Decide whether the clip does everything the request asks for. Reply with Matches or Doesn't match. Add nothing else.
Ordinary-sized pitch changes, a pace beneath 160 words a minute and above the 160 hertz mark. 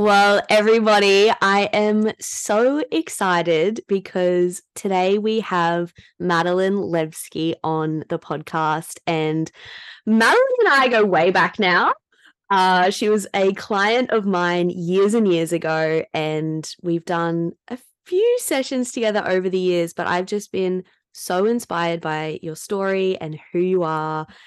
Matches